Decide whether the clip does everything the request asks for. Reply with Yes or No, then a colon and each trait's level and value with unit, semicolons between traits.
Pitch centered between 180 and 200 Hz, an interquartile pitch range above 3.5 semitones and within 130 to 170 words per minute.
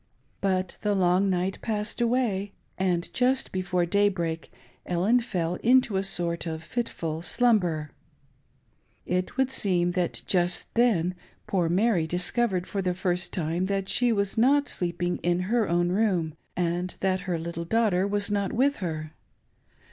No: medium, 185 Hz; average, 3.1 semitones; average, 155 wpm